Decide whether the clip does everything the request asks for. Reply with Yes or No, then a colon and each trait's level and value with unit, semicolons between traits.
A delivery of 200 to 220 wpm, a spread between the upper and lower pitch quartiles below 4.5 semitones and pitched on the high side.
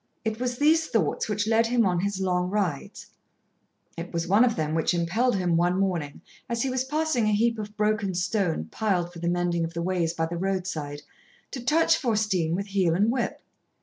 No: fast, 205 wpm; average, 4.8 semitones; high, 195 Hz